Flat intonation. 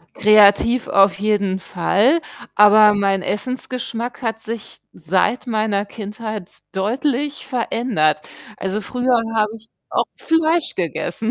No: average, 3.6 semitones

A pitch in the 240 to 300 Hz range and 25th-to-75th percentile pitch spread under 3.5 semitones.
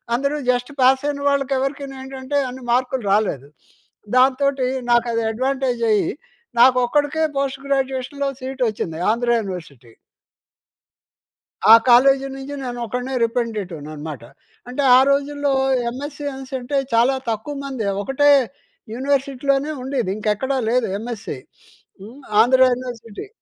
Yes: very high, 260 Hz; average, 3.0 semitones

